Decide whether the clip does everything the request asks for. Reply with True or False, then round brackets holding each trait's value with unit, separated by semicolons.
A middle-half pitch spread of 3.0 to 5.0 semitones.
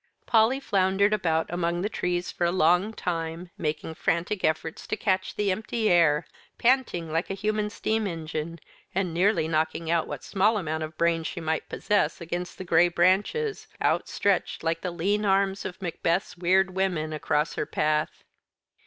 True (3.3 semitones)